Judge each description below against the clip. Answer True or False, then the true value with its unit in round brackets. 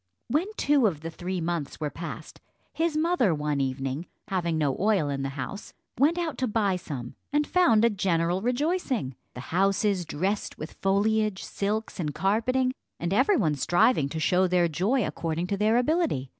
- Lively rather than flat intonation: True (7.0 semitones)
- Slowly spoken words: False (175 wpm)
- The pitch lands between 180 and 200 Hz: True (190 Hz)